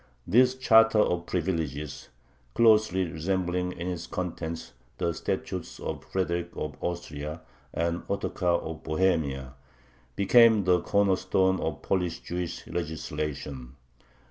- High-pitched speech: No, very low, 85 Hz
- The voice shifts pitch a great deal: No, average, 2.9 semitones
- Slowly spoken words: Yes, slow, 115 wpm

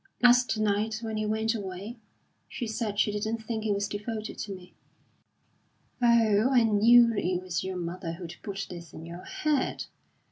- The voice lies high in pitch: Yes, high, 215 Hz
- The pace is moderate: Yes, average, 170 wpm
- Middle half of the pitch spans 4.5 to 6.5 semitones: No, average, 3.2 semitones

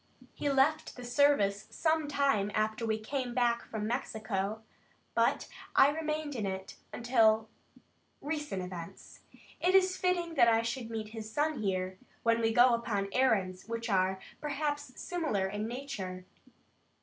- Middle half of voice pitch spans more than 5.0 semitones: Yes, wide, 5.4 semitones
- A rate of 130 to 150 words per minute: Yes, average, 145 wpm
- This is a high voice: Yes, high, 230 Hz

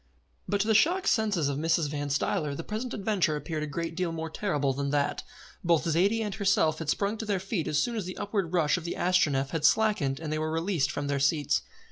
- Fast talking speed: Yes, fast, 235 wpm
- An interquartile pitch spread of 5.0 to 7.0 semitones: Yes, average, 5.3 semitones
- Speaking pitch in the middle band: Yes, medium, 165 Hz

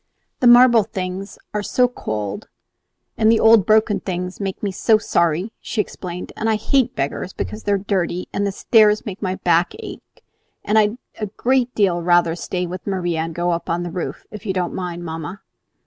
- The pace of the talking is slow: No, average, 195 wpm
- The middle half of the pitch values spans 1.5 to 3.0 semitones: No, average, 3.7 semitones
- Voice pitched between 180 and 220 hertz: Yes, high, 190 Hz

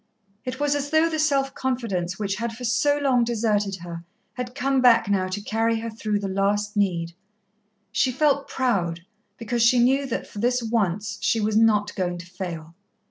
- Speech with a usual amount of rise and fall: Yes, average, 4.3 semitones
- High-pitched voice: Yes, high, 225 Hz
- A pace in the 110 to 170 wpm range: No, average, 190 wpm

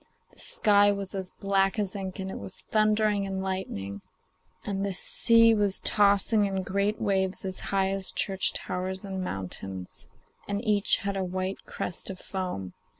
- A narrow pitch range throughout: Yes, narrow, 1.4 semitones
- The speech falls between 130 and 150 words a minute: No, average, 160 wpm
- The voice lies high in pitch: Yes, high, 195 Hz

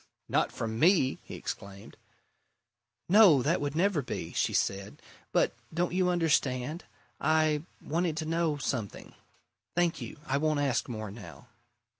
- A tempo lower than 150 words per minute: Yes, average, 140 wpm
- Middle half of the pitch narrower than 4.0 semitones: No, average, 5.1 semitones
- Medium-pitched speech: Yes, medium, 150 Hz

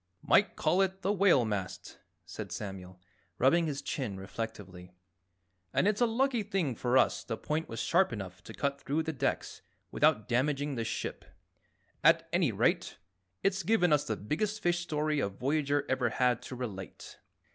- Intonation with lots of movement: Yes, wide, 7.6 semitones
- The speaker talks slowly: No, average, 165 wpm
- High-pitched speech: No, medium, 140 Hz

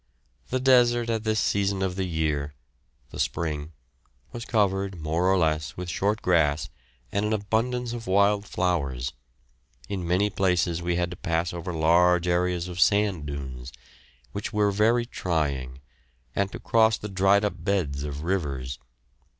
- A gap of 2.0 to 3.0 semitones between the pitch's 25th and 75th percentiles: No, average, 4.2 semitones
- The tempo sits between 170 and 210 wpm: No, average, 155 wpm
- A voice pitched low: Yes, very low, 90 Hz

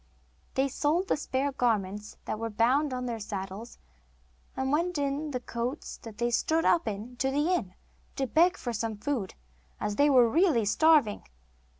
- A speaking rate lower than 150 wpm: No, average, 170 wpm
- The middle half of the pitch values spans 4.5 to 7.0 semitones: Yes, average, 4.8 semitones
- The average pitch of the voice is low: No, very high, 250 Hz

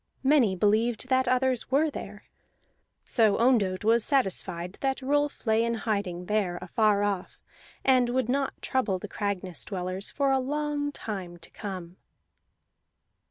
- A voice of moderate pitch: No, high, 225 Hz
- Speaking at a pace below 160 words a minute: Yes, average, 140 wpm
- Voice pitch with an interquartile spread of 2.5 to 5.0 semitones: No, wide, 5.4 semitones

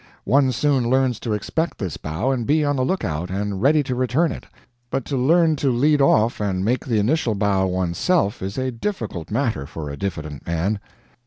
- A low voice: Yes, low, 120 Hz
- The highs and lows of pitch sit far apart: Yes, wide, 6.2 semitones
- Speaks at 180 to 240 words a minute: Yes, average, 200 wpm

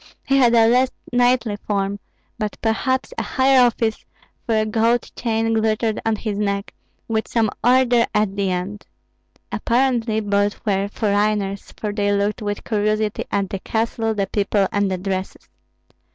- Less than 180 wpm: Yes, average, 155 wpm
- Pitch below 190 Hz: No, high, 215 Hz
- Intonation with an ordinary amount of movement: No, narrow, 2.3 semitones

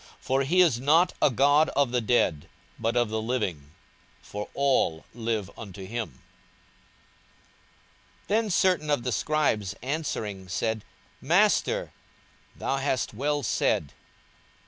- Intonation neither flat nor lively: No, wide, 5.7 semitones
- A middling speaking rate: No, slow, 130 wpm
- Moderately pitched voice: No, low, 125 Hz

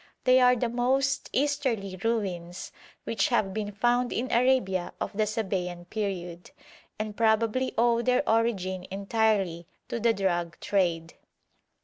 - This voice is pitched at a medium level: No, high, 215 Hz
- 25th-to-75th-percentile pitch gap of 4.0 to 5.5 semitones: Yes, average, 4.3 semitones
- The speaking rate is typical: No, slow, 130 wpm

